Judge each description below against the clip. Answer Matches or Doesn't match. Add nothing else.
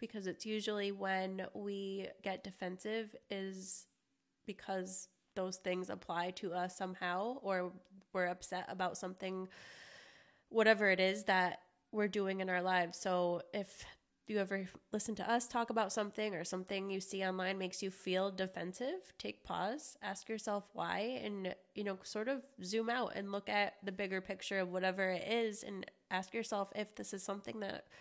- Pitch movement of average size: Doesn't match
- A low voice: Doesn't match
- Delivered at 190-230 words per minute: Doesn't match